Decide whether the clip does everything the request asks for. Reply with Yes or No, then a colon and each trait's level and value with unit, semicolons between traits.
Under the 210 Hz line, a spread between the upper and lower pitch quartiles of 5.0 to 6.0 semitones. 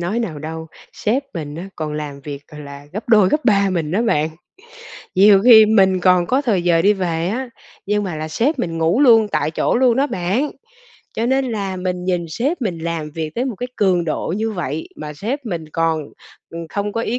Yes: medium, 185 Hz; wide, 5.6 semitones